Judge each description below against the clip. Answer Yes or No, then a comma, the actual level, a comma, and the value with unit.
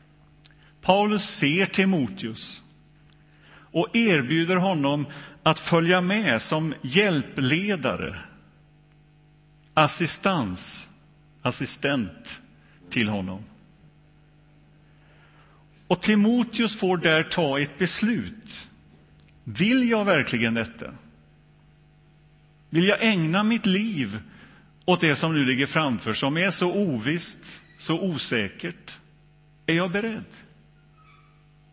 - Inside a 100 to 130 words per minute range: No, slow, 85 wpm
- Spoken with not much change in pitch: No, average, 3.9 semitones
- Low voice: No, medium, 155 Hz